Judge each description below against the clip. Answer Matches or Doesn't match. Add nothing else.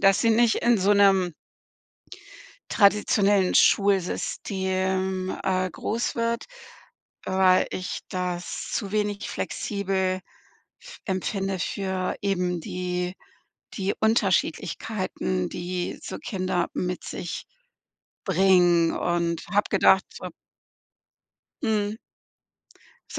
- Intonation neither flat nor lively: Doesn't match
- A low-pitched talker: Doesn't match